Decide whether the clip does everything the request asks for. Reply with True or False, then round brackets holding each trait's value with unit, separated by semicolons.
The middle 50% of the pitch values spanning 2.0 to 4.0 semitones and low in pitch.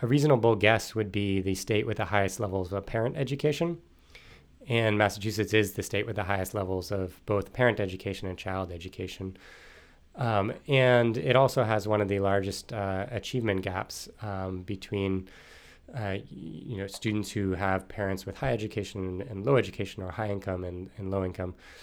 True (2.5 semitones; 100 Hz)